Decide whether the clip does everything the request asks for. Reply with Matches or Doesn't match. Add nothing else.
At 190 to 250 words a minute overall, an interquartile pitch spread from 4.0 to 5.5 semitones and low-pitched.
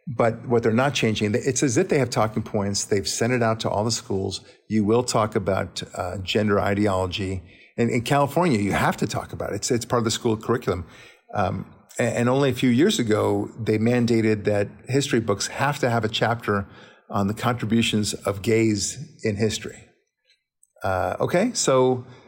Doesn't match